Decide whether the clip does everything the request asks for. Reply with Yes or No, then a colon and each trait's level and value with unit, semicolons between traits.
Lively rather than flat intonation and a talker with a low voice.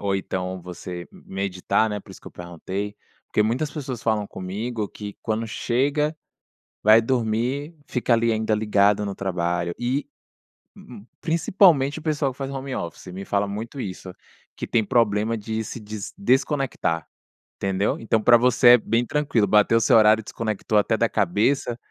No: average, 3.9 semitones; low, 110 Hz